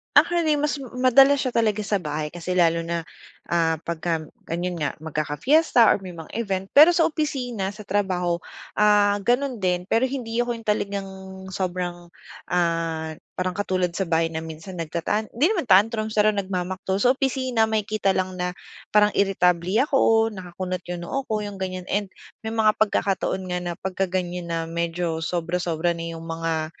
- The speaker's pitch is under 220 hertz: Yes, high, 190 Hz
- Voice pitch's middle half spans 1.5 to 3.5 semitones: No, average, 4.3 semitones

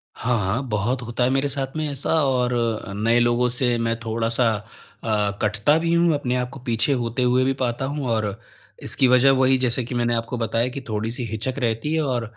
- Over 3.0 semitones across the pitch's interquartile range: No, narrow, 2.4 semitones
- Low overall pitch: Yes, low, 120 Hz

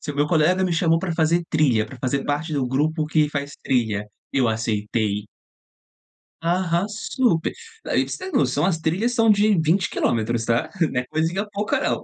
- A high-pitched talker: No, medium, 155 Hz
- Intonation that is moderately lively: No, wide, 5.8 semitones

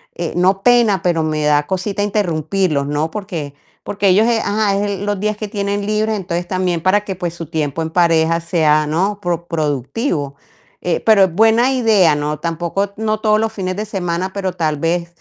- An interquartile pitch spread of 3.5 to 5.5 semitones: Yes, average, 4.0 semitones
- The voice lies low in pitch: No, medium, 185 Hz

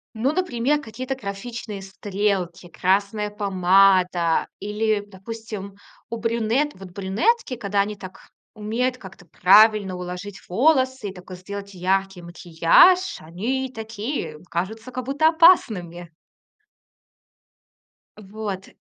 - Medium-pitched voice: No, high, 205 Hz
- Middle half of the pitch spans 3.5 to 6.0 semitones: Yes, average, 3.8 semitones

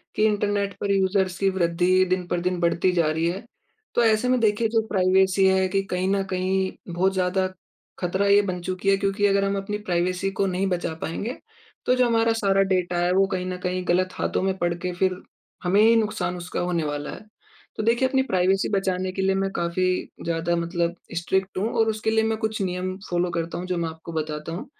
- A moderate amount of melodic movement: No, narrow, 2.0 semitones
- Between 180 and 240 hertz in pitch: Yes, medium, 185 Hz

